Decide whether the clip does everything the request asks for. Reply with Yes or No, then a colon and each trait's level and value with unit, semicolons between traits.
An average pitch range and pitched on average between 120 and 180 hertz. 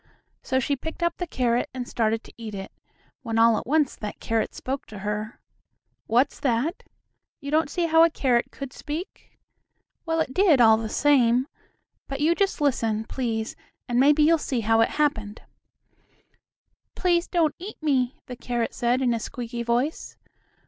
No: average, 4.9 semitones; very high, 255 Hz